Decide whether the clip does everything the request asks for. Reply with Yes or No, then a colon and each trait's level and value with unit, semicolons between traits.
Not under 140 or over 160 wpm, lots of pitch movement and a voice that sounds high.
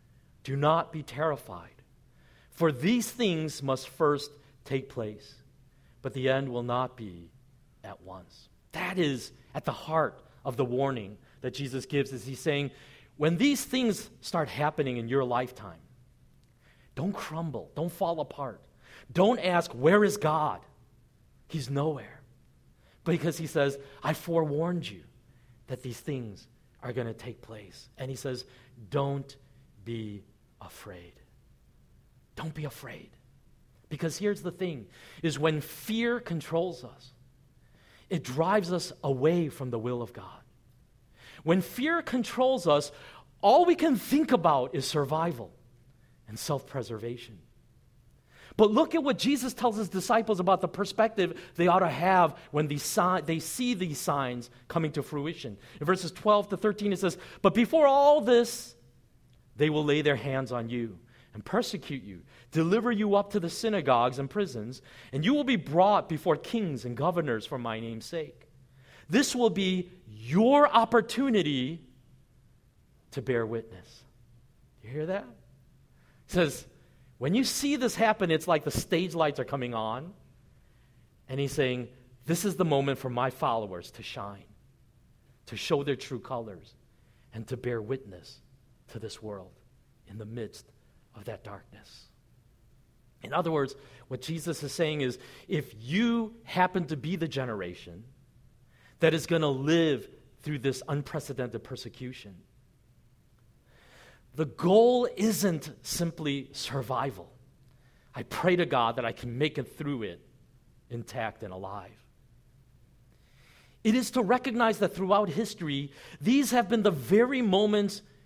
No: average, 145 wpm; wide, 6.3 semitones; medium, 140 Hz